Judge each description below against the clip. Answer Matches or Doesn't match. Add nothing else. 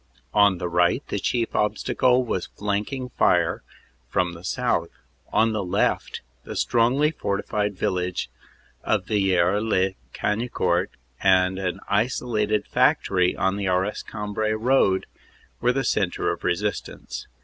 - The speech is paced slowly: Matches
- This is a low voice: Matches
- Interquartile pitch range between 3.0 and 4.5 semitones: Matches